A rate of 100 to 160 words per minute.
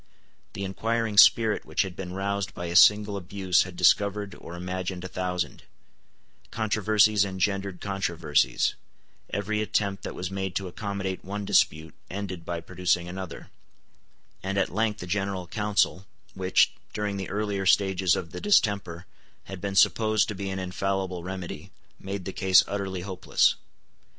Yes: average, 150 wpm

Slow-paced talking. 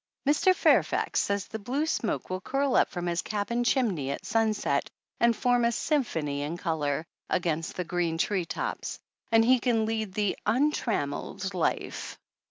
No: average, 160 wpm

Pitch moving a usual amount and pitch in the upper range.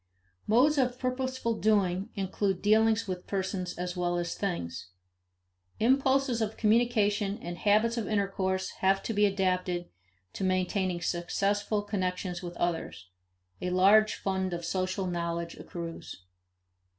Yes: average, 3.2 semitones; high, 195 Hz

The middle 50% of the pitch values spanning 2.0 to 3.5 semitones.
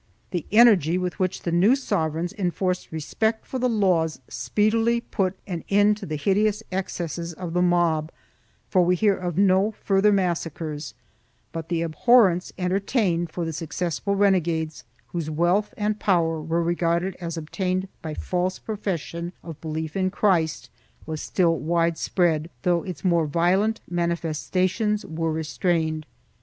Yes: average, 3.0 semitones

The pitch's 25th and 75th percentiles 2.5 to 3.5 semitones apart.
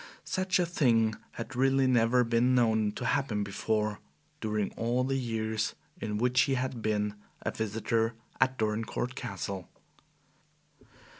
Yes: average, 2.8 semitones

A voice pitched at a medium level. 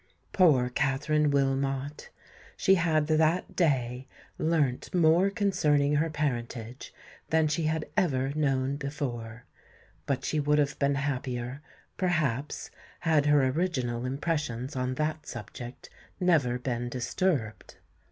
Yes: medium, 145 Hz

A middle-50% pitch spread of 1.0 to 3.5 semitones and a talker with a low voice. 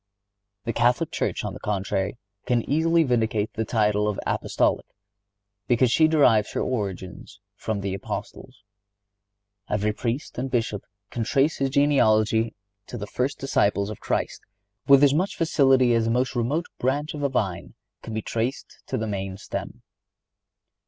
No: average, 4.4 semitones; low, 115 Hz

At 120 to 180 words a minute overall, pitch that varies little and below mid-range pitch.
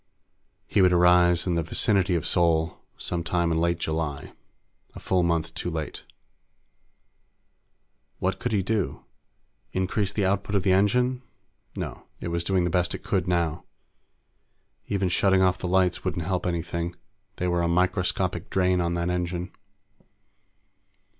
Yes: average, 150 wpm; narrow, 1.7 semitones; very low, 90 Hz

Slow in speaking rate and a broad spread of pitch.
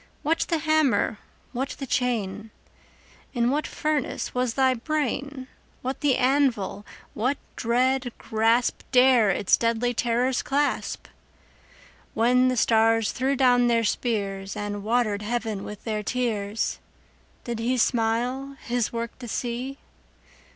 No: slow, 130 wpm; average, 2.7 semitones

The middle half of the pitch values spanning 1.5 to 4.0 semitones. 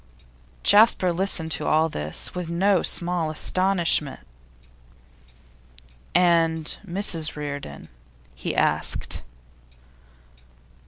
Yes: average, 2.9 semitones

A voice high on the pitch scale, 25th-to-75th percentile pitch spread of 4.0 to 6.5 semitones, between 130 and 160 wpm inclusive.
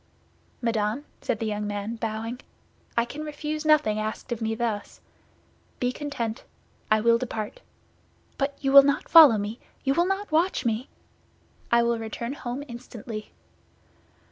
Yes: high, 235 Hz; average, 4.5 semitones; average, 145 wpm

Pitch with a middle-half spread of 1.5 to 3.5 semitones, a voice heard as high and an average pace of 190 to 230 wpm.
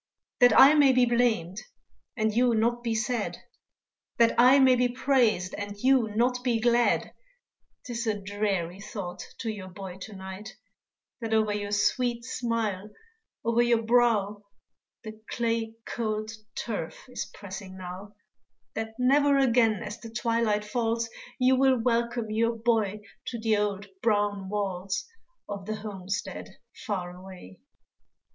No: average, 2.8 semitones; high, 220 Hz; average, 140 wpm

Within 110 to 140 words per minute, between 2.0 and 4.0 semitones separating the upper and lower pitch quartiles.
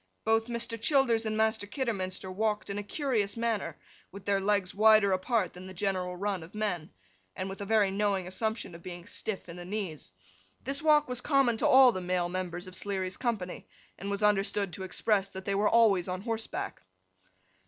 No: average, 195 wpm; average, 3.1 semitones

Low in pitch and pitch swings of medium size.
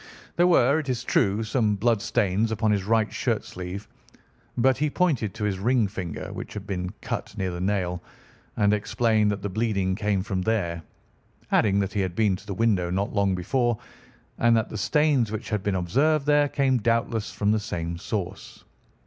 Yes: low, 105 Hz; average, 3.4 semitones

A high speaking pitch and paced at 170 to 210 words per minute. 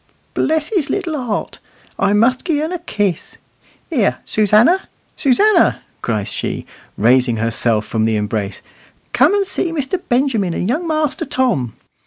No: high, 245 Hz; average, 145 wpm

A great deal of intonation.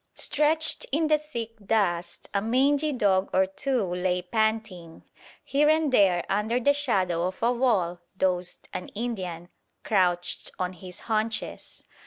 Yes: wide, 5.8 semitones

